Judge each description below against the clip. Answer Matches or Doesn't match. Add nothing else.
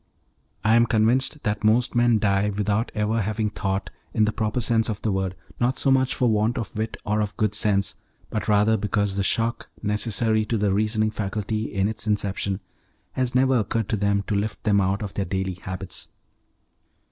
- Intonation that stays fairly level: Matches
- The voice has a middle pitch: Doesn't match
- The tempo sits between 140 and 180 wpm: Doesn't match